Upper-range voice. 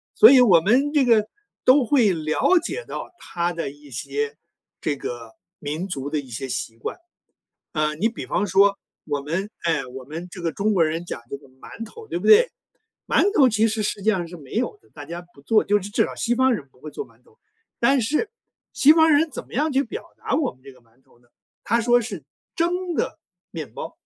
Yes: high, 195 Hz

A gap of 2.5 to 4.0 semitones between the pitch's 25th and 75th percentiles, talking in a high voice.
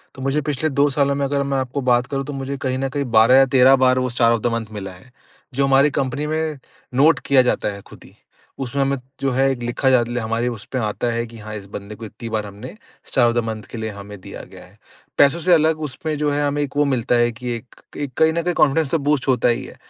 No: average, 3.2 semitones; low, 130 Hz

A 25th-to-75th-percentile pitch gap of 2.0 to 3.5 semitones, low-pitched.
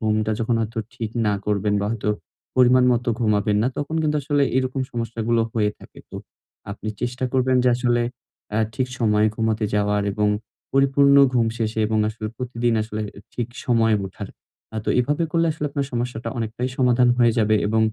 Yes: average, 2.8 semitones; low, 115 Hz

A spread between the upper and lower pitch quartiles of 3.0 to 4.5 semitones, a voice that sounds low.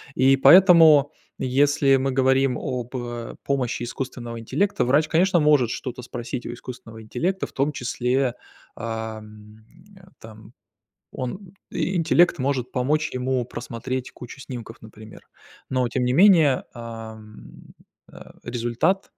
Yes: average, 3.5 semitones; low, 130 Hz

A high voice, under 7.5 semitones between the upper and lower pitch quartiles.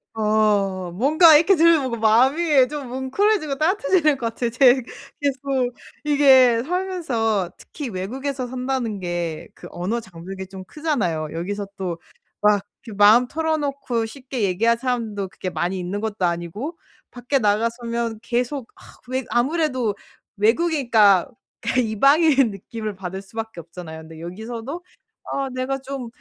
Yes: high, 235 Hz; wide, 5.5 semitones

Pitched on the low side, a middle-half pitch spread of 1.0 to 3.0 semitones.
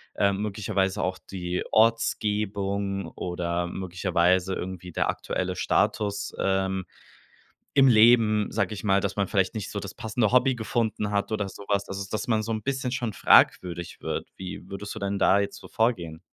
Yes: low, 100 Hz; narrow, 2.5 semitones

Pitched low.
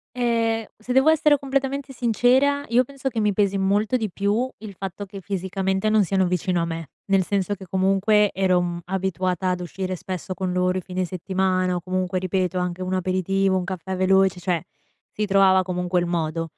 No: high, 190 Hz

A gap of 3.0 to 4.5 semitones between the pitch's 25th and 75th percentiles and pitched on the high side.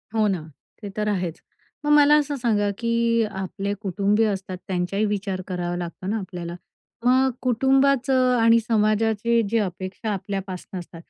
Yes: average, 3.7 semitones; high, 210 Hz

